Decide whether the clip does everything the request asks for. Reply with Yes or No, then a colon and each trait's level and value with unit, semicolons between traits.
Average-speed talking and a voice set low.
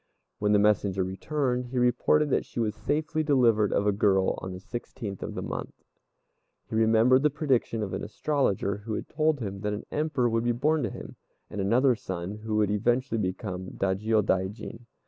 Yes: average, 190 wpm; low, 110 Hz